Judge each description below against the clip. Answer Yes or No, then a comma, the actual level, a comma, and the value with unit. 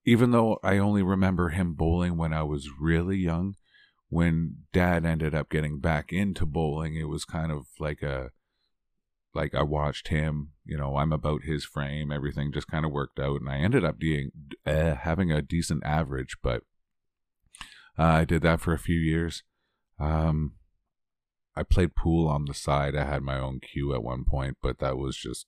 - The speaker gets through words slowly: No, average, 190 wpm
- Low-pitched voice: Yes, very low, 75 Hz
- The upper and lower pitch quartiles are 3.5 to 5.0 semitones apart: No, narrow, 2.5 semitones